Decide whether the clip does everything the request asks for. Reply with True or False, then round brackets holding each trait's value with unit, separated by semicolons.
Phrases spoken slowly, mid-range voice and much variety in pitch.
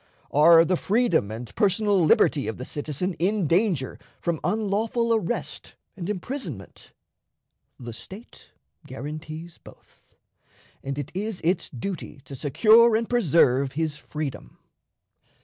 True (120 wpm; 170 Hz; 6.4 semitones)